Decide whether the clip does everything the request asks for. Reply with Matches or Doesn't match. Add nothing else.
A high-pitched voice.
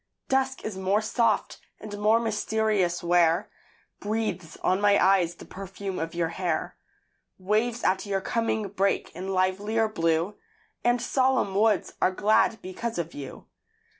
Matches